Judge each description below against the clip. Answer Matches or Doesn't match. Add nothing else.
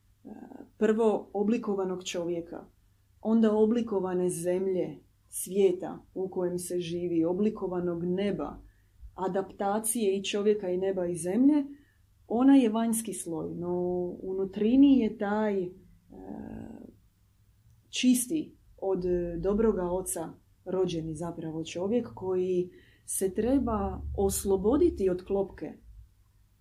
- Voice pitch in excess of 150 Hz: Matches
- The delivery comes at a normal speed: Doesn't match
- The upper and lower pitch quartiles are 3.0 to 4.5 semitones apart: Matches